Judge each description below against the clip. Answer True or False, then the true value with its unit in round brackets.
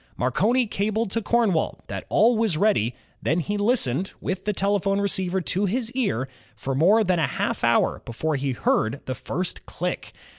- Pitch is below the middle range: False (190 Hz)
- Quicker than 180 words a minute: False (175 wpm)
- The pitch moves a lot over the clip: True (6.9 semitones)